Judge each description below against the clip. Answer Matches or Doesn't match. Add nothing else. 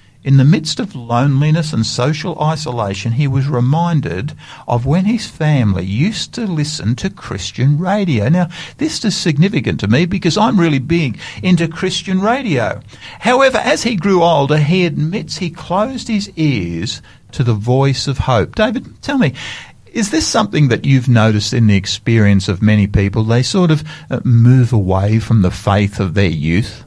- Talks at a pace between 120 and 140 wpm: Doesn't match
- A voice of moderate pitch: Matches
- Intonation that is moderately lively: Doesn't match